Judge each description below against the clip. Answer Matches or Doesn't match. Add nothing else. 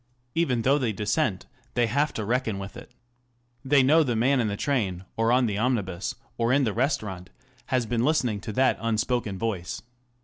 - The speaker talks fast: Doesn't match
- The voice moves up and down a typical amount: Matches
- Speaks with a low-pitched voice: Matches